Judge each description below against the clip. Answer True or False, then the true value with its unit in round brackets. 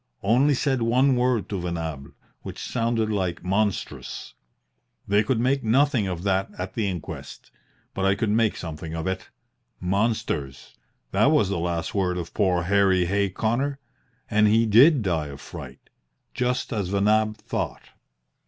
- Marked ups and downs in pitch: False (4.2 semitones)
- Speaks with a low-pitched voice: True (100 Hz)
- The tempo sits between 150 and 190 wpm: True (155 wpm)